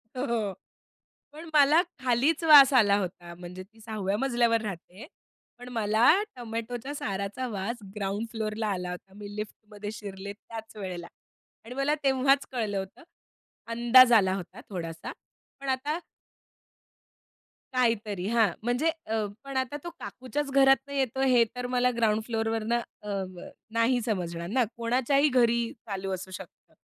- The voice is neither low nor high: No, high, 230 Hz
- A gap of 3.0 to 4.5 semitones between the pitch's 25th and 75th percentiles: Yes, average, 4.1 semitones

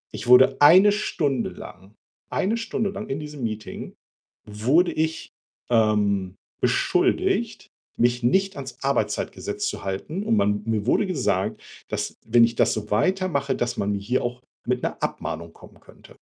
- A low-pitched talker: Yes, low, 125 Hz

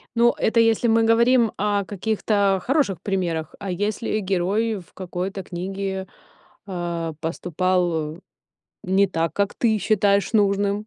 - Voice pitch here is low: No, high, 195 Hz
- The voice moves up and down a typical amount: Yes, average, 3.1 semitones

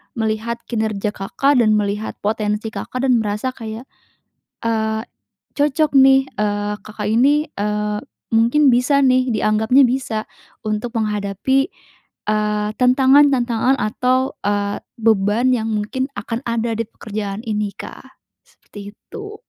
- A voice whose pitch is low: No, high, 225 Hz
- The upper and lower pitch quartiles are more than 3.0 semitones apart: Yes, average, 3.4 semitones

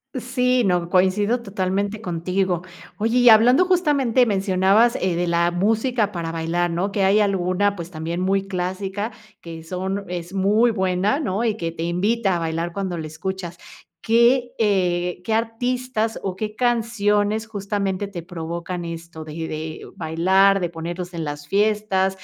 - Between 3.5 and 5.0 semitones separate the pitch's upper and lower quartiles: Yes, average, 3.9 semitones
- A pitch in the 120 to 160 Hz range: No, high, 190 Hz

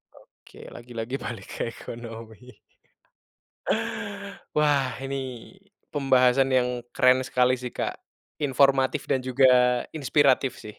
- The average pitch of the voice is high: No, low, 125 Hz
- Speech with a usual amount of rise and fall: No, narrow, 1.7 semitones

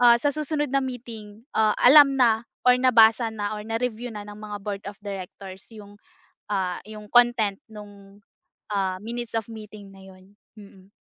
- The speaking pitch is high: Yes, high, 215 Hz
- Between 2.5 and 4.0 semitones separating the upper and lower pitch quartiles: Yes, average, 2.9 semitones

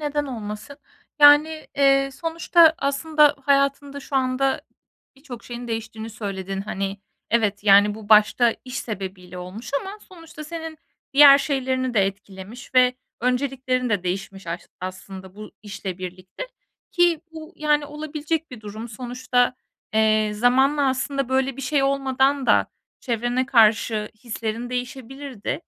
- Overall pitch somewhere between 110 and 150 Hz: No, very high, 250 Hz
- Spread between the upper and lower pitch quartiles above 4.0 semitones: Yes, average, 4.9 semitones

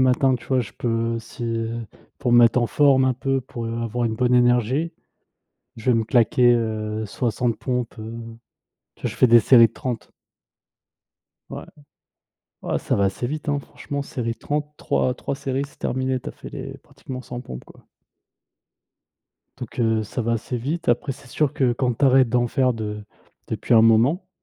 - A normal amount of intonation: No, narrow, 2.3 semitones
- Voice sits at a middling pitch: No, low, 120 Hz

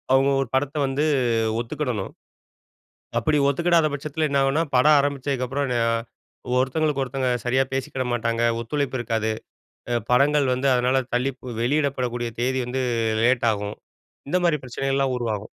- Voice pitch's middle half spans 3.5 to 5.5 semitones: No, narrow, 2.5 semitones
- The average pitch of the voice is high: No, low, 135 Hz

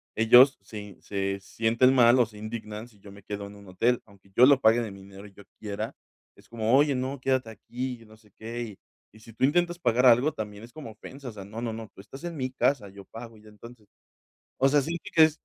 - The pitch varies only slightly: No, average, 3.7 semitones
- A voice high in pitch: No, low, 115 Hz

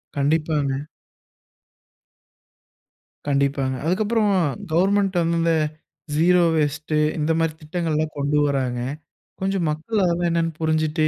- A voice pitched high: No, medium, 160 Hz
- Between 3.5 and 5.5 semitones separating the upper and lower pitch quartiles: No, average, 2.8 semitones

